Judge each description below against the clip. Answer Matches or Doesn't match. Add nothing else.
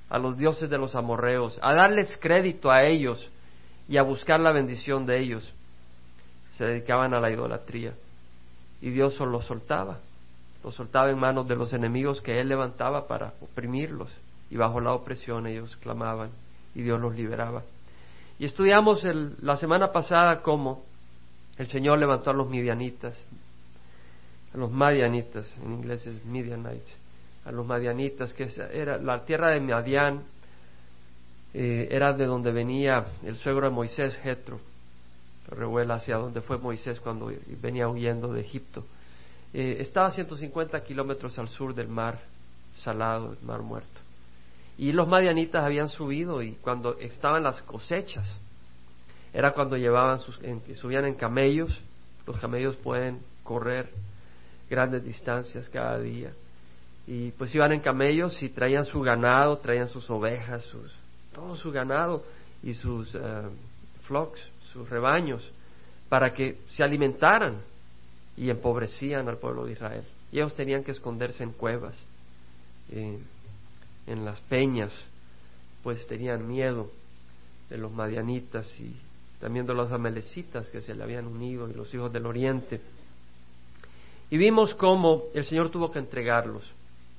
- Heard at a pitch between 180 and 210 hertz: Doesn't match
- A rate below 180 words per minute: Matches